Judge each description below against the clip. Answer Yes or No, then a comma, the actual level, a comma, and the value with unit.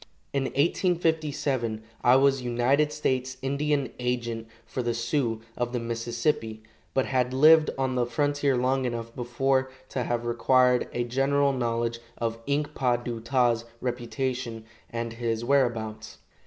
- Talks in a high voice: No, low, 125 Hz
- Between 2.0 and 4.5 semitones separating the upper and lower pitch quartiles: Yes, narrow, 2.6 semitones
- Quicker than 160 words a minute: No, average, 140 wpm